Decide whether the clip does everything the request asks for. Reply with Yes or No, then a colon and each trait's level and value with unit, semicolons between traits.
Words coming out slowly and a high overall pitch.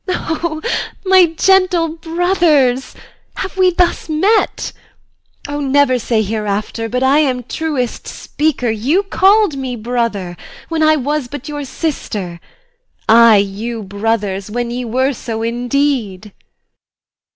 Yes: slow, 120 wpm; very high, 260 Hz